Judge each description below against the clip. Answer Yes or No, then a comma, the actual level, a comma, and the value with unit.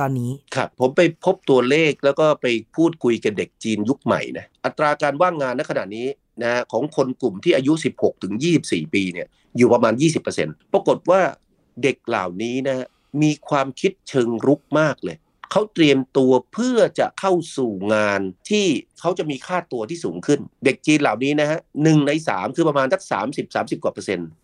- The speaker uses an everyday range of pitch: Yes, average, 4.5 semitones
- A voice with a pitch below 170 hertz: Yes, medium, 140 Hz